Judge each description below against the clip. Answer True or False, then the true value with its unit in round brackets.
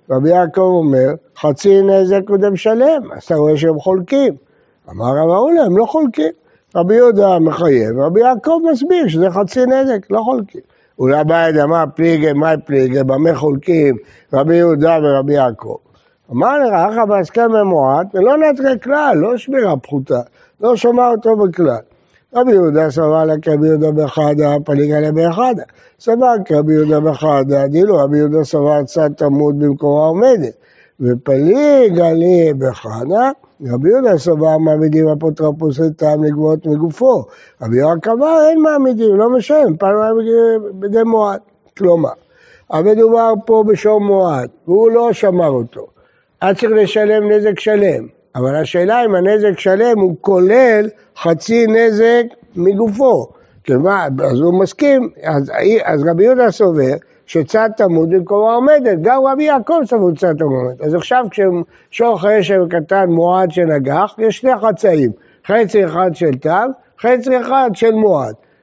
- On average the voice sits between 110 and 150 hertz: False (190 Hz)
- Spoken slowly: False (145 wpm)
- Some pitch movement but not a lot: False (6.6 semitones)